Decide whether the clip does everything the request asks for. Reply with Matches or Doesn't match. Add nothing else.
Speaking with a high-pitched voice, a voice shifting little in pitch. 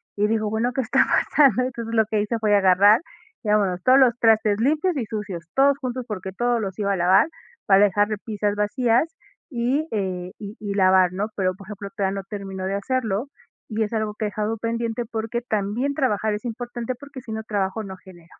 Doesn't match